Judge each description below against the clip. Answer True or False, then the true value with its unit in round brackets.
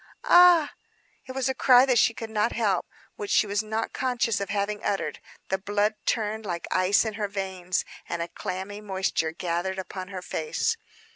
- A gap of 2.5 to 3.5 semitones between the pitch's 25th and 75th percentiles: True (3.2 semitones)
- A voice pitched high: True (205 Hz)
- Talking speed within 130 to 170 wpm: False (185 wpm)